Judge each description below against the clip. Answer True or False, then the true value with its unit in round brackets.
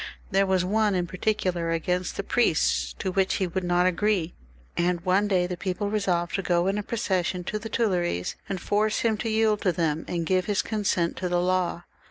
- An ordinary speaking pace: False (210 wpm)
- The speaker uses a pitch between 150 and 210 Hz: True (185 Hz)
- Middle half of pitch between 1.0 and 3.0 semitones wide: True (2.7 semitones)